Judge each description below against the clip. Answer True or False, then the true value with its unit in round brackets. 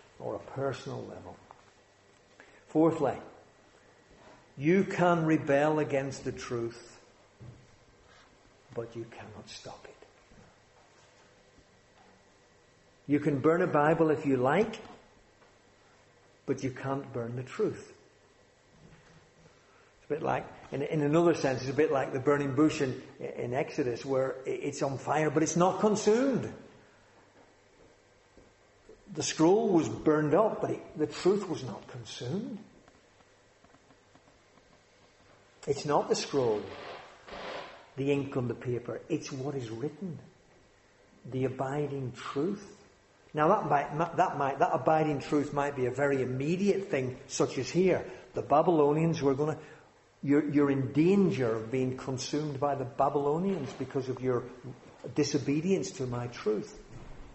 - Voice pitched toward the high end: False (140 Hz)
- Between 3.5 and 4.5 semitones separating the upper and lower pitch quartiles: True (4.2 semitones)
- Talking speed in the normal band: False (130 wpm)